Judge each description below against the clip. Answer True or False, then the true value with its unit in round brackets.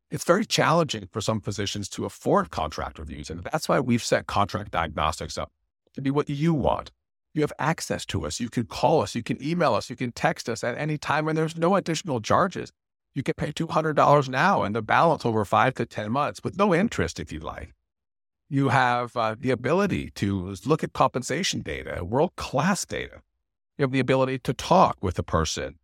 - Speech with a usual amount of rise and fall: False (7.0 semitones)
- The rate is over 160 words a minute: True (205 wpm)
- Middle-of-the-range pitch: False (120 Hz)